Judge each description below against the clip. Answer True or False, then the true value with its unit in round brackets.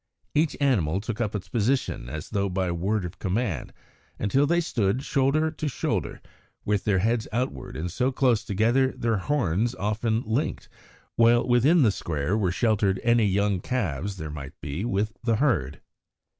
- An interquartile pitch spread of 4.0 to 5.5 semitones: True (4.8 semitones)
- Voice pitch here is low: True (110 Hz)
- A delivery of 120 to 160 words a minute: False (170 wpm)